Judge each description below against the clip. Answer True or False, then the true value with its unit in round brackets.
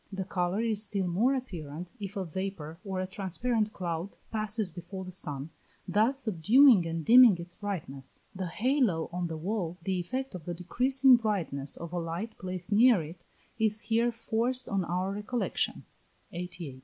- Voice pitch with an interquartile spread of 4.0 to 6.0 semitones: True (4.4 semitones)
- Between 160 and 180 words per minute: True (170 wpm)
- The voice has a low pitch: False (190 Hz)